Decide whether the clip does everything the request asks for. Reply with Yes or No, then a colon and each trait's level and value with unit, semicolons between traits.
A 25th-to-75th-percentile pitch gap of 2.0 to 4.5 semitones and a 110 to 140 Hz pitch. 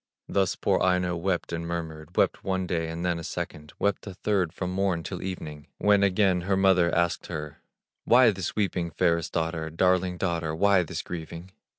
No: narrow, 2.4 semitones; very low, 90 Hz